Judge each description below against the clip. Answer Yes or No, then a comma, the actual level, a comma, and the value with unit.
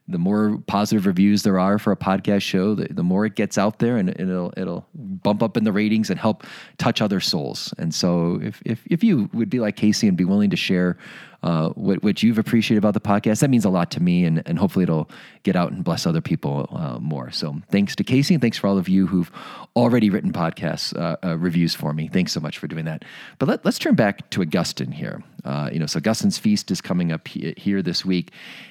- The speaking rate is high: Yes, fast, 240 wpm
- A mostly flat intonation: No, average, 3.7 semitones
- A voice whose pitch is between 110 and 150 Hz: No, low, 100 Hz